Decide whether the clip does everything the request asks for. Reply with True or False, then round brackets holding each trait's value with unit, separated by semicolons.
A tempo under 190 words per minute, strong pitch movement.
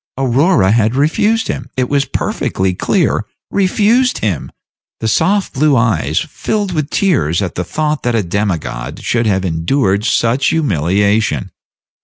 True (140 wpm; 8.1 semitones)